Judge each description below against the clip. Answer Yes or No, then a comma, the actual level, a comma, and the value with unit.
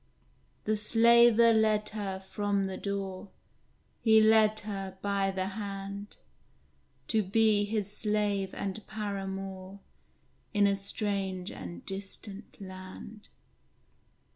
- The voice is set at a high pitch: Yes, high, 200 Hz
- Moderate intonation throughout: No, narrow, 1.8 semitones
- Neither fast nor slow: No, slow, 105 wpm